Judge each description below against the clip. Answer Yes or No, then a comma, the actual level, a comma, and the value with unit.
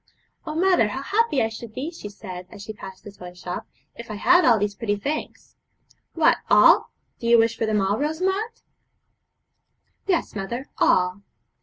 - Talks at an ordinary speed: Yes, average, 175 wpm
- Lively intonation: Yes, wide, 7.2 semitones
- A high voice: Yes, high, 225 Hz